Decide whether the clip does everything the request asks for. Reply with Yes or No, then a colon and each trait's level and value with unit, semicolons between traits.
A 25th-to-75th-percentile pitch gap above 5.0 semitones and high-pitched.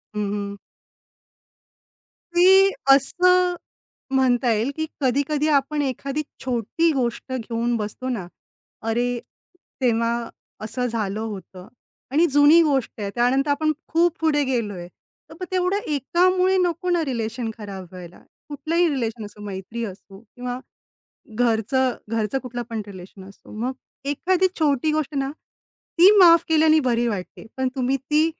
Yes: wide, 5.5 semitones; very high, 255 Hz